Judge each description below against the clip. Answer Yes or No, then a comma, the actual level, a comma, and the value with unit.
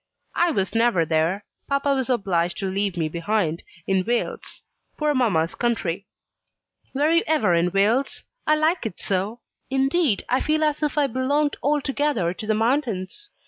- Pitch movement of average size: No, wide, 7.5 semitones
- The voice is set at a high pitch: Yes, high, 235 Hz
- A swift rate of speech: No, average, 160 wpm